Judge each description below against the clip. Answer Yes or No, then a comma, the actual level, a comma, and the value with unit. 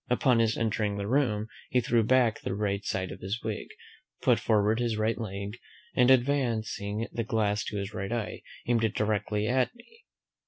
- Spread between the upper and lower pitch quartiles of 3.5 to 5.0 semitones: No, narrow, 2.5 semitones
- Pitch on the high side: No, low, 110 Hz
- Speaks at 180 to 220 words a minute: Yes, average, 185 wpm